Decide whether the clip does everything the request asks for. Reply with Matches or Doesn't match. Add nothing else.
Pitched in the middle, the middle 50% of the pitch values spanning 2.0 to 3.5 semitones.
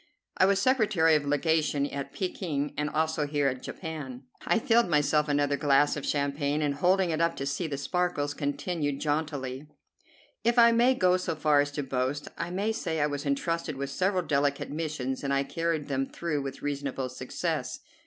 Matches